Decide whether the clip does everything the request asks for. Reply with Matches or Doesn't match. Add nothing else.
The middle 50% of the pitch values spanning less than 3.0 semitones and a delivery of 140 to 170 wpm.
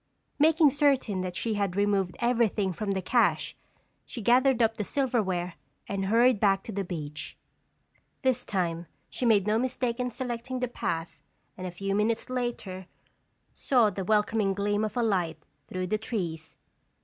Doesn't match